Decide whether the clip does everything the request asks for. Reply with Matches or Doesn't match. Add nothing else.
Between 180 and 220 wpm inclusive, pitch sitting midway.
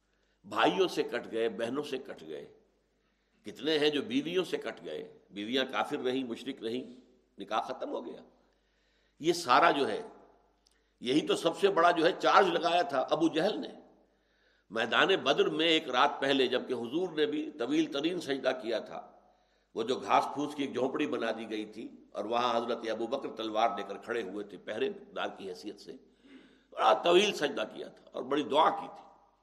Matches